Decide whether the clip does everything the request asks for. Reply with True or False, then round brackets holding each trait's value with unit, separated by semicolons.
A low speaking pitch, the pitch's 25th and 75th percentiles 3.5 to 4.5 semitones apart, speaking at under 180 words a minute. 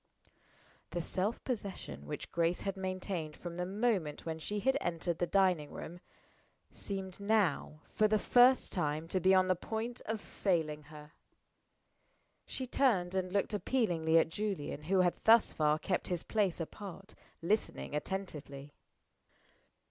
False (185 Hz; 4.1 semitones; 150 wpm)